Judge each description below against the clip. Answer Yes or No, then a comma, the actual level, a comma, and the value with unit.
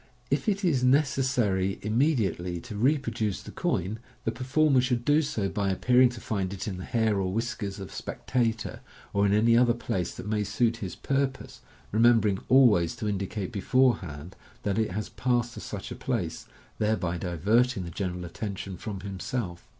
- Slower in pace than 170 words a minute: No, average, 180 wpm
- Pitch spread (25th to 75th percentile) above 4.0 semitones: Yes, average, 4.4 semitones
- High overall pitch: No, low, 110 Hz